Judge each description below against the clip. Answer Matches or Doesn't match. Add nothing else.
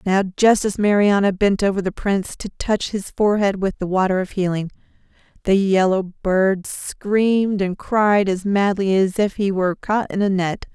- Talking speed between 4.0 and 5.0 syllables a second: Matches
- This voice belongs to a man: Doesn't match